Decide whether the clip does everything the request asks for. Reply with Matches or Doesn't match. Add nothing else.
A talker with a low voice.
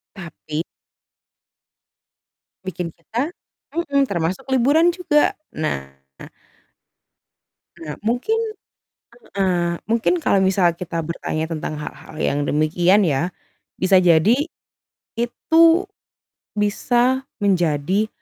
Doesn't match